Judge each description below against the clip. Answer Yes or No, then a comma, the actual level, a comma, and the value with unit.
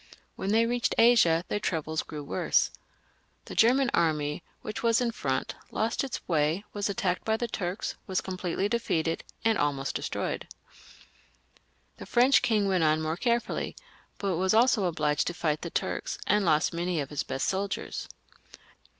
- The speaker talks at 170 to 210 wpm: No, average, 160 wpm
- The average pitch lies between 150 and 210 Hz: Yes, medium, 185 Hz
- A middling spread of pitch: No, wide, 5.9 semitones